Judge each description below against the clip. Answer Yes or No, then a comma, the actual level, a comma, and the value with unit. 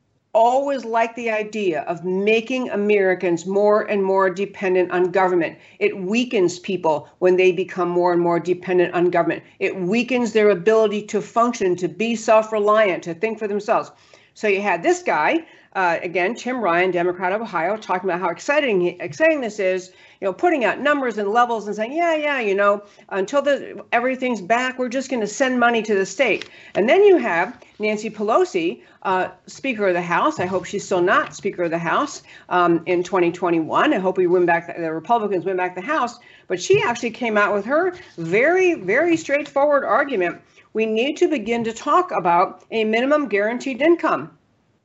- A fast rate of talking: No, average, 185 wpm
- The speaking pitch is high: Yes, high, 210 Hz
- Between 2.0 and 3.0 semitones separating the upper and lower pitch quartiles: No, average, 5.3 semitones